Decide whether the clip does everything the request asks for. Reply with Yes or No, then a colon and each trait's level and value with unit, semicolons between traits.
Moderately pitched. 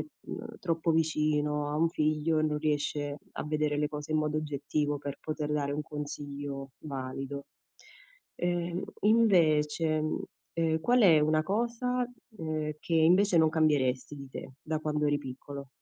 Yes: medium, 150 Hz